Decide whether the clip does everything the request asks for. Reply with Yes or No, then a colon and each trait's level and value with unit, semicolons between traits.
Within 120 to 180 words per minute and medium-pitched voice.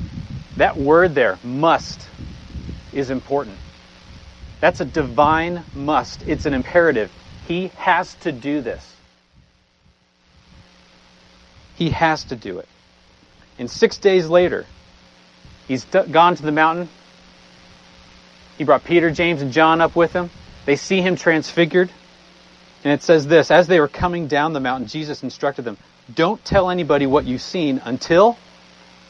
Yes: average, 140 wpm; medium, 145 Hz